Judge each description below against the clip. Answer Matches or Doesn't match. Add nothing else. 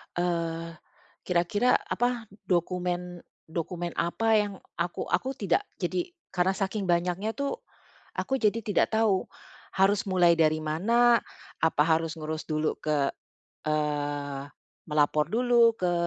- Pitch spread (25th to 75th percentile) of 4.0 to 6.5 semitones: Matches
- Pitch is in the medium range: Matches